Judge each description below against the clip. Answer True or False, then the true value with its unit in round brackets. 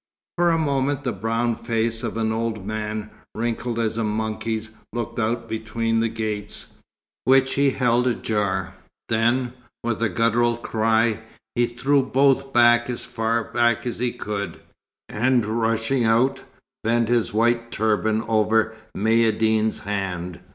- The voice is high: False (115 Hz)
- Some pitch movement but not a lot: False (1.5 semitones)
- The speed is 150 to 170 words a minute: False (135 wpm)